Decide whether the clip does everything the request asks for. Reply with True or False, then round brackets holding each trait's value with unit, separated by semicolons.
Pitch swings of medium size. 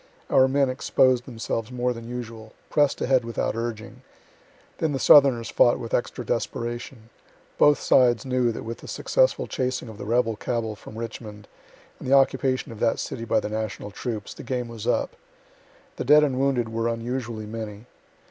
False (2.3 semitones)